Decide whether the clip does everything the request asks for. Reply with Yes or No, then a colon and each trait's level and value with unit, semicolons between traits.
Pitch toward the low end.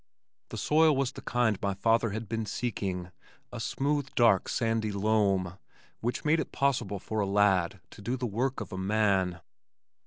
Yes: low, 110 Hz